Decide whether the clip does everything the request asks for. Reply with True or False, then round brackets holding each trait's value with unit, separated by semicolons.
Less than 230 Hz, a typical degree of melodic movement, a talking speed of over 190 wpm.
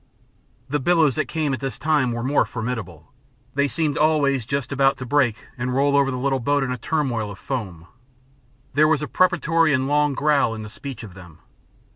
True (135 Hz; 3.7 semitones; 200 wpm)